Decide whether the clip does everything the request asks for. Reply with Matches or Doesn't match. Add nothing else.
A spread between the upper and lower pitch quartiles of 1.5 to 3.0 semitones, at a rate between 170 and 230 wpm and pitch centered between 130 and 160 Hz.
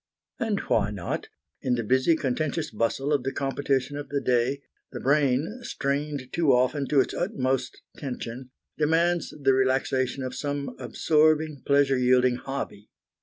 Doesn't match